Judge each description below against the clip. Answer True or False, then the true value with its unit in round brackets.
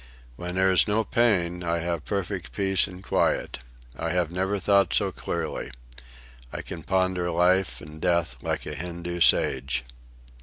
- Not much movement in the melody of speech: True (2.1 semitones)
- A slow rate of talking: False (155 wpm)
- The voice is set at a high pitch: False (90 Hz)